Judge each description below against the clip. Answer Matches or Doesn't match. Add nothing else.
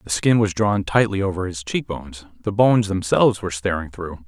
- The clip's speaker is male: Matches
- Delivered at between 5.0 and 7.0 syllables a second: Matches